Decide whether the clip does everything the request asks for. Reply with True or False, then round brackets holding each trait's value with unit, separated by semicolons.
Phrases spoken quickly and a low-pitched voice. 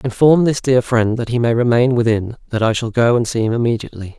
True (245 wpm; 120 Hz)